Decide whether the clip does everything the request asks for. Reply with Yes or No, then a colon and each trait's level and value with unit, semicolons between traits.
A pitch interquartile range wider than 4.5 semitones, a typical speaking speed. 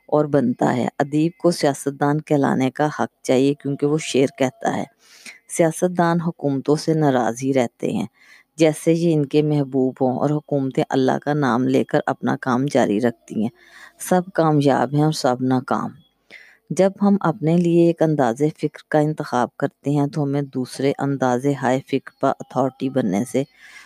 No: average, 2.9 semitones; average, 170 wpm